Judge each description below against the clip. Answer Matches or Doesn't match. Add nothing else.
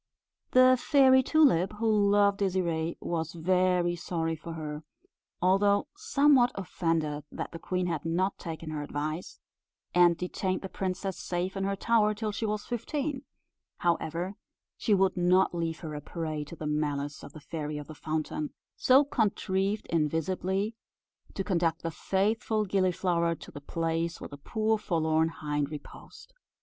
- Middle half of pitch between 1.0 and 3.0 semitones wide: Doesn't match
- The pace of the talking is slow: Doesn't match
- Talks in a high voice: Doesn't match